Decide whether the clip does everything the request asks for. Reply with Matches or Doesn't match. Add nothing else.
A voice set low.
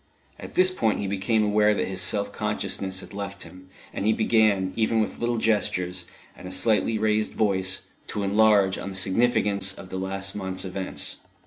Matches